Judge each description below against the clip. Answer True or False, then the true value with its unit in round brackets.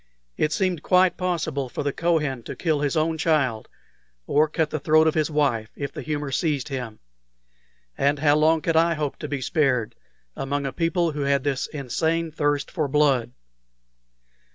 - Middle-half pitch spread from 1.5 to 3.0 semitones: True (2.4 semitones)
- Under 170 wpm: False (175 wpm)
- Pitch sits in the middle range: True (150 Hz)